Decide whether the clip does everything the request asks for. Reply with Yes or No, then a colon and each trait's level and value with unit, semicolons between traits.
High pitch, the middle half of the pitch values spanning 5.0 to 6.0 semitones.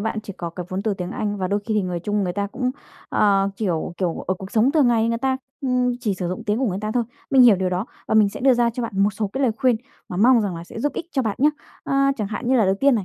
No: high, 210 Hz; average, 4.2 semitones